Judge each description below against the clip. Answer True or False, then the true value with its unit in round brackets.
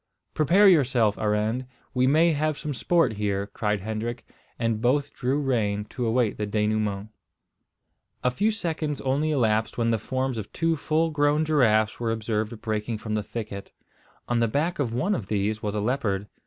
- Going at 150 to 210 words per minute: True (175 wpm)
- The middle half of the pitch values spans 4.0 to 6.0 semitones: True (5.3 semitones)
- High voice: False (115 Hz)